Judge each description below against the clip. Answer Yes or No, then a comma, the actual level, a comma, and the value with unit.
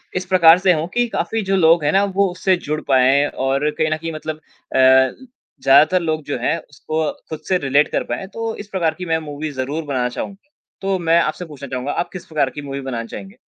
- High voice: No, medium, 155 Hz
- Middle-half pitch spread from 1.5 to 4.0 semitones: No, average, 4.8 semitones